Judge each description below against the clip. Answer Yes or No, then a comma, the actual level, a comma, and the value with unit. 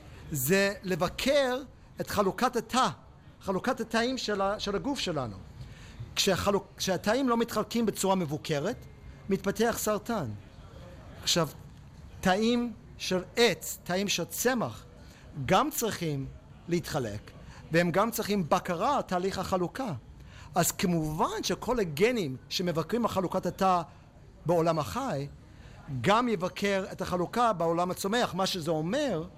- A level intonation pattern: No, average, 4.5 semitones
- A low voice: No, medium, 185 Hz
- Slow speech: No, average, 115 wpm